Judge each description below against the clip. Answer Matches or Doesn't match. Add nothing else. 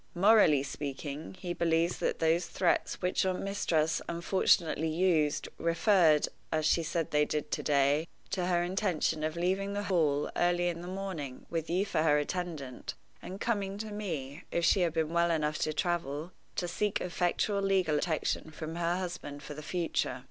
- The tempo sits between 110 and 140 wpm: Doesn't match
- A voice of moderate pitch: Matches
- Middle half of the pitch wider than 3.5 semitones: Doesn't match